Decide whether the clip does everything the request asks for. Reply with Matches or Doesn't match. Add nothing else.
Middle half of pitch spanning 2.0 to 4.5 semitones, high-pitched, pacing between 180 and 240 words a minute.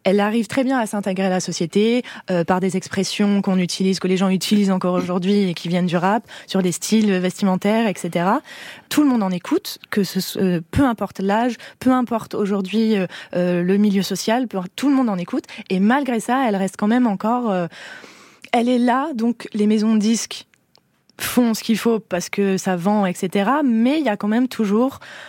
Matches